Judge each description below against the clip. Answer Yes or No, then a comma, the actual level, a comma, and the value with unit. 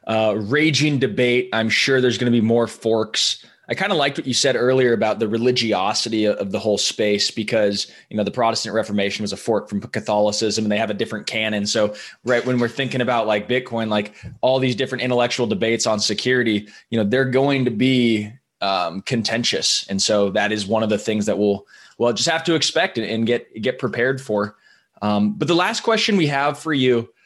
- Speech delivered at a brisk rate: Yes, fast, 210 wpm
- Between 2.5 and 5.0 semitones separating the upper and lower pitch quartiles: Yes, average, 3.2 semitones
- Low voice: Yes, low, 115 Hz